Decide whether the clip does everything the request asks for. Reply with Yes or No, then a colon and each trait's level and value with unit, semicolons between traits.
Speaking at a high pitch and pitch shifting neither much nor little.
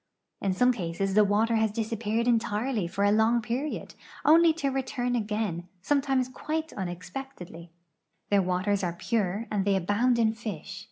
Yes: high, 220 Hz; average, 4.1 semitones